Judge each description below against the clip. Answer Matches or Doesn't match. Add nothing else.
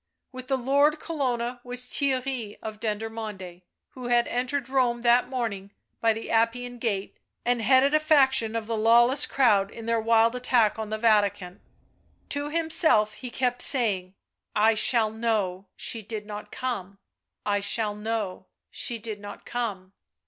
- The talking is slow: Doesn't match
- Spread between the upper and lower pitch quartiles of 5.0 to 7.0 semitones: Doesn't match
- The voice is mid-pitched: Doesn't match